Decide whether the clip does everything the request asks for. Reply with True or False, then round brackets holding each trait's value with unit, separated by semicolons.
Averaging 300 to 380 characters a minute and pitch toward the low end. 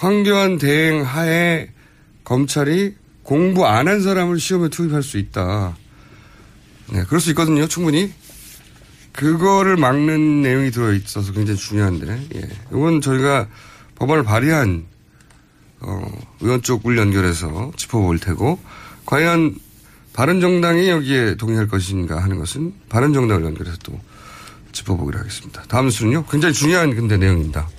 True (305 characters per minute; 130 Hz)